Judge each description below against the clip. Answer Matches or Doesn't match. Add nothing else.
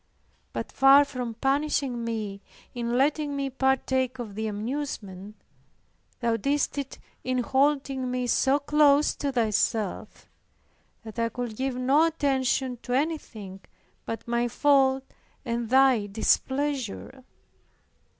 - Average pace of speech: Doesn't match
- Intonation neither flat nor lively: Matches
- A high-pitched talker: Matches